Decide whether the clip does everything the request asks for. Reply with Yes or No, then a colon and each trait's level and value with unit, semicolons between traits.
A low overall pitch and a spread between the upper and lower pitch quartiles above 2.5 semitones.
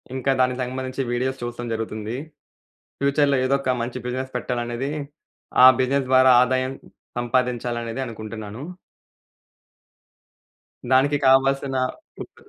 No: low, 130 Hz; narrow, 1.8 semitones